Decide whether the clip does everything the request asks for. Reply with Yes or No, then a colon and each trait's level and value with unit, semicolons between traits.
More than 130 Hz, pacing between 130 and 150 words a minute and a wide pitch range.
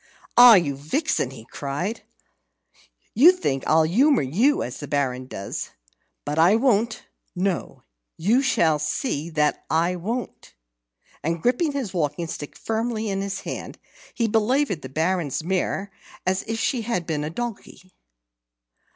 Yes: medium, 185 Hz; average, 140 wpm; wide, 7.2 semitones